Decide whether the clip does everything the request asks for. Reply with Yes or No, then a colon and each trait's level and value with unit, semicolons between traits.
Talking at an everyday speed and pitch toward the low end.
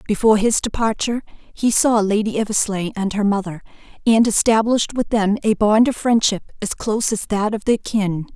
No: average, 180 wpm; high, 215 Hz